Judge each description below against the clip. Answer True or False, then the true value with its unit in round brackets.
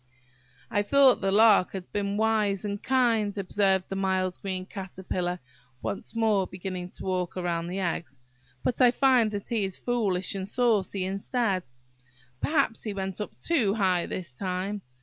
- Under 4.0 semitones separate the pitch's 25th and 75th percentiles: True (2.9 semitones)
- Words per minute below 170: True (160 wpm)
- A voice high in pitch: True (195 Hz)